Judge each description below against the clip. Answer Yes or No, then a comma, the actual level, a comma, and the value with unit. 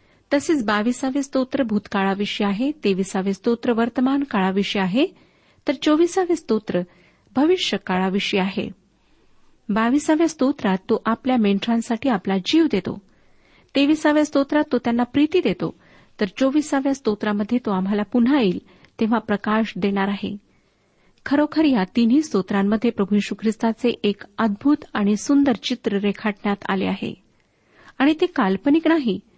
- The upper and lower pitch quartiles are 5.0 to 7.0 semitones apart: Yes, wide, 5.5 semitones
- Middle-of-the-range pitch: No, high, 230 Hz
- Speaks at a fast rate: No, average, 110 wpm